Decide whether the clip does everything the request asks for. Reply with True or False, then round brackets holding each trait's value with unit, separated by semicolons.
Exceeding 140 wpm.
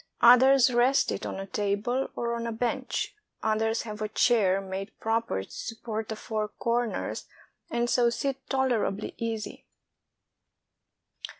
False (135 wpm)